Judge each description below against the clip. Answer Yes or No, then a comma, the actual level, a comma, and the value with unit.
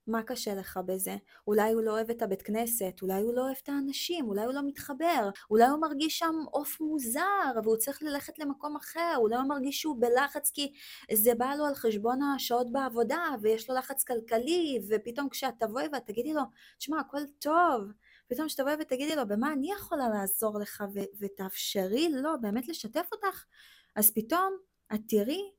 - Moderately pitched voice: No, very high, 265 Hz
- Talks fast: Yes, fast, 185 wpm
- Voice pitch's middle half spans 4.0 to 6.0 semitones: Yes, average, 5.2 semitones